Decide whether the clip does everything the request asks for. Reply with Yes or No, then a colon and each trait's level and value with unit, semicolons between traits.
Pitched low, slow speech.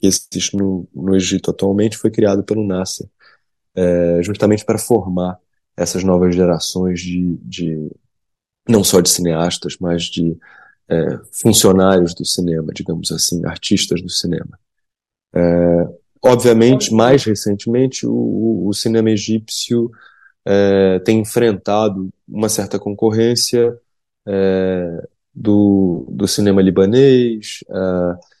Yes: very low, 95 Hz; slow, 115 wpm